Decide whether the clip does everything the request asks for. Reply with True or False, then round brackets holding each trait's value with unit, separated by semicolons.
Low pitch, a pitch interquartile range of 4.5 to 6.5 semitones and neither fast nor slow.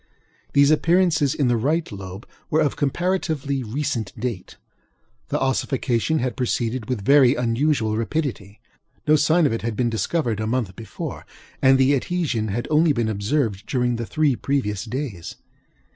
True (130 Hz; 4.8 semitones; 155 wpm)